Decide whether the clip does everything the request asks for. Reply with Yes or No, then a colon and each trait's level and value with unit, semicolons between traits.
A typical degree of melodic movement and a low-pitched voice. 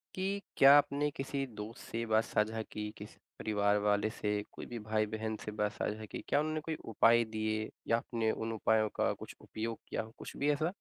Yes: average, 3.9 semitones; low, 110 Hz